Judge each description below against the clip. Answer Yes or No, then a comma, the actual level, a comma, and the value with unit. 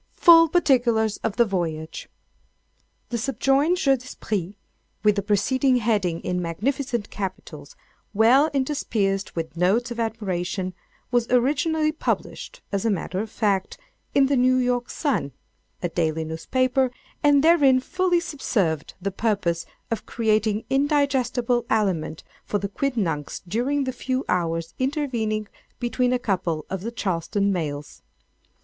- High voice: Yes, high, 225 Hz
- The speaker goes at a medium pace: No, slow, 130 wpm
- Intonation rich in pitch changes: Yes, wide, 6.0 semitones